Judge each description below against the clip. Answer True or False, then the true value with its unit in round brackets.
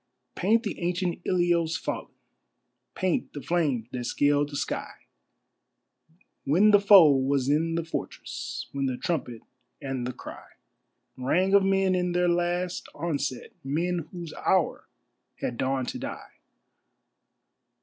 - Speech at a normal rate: False (130 wpm)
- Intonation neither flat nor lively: True (4.4 semitones)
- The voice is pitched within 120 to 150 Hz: False (165 Hz)